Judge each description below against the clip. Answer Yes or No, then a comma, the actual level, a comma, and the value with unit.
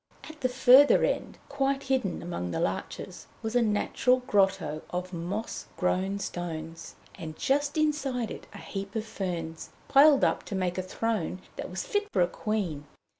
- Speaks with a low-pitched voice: No, high, 200 Hz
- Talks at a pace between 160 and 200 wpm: Yes, average, 170 wpm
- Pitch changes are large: Yes, wide, 6.8 semitones